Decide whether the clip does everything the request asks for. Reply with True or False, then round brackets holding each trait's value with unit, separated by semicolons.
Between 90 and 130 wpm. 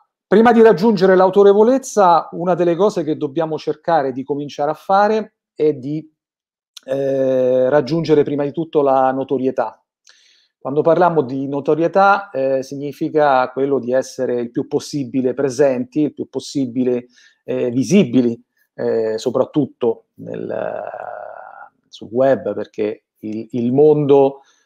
True (125 wpm)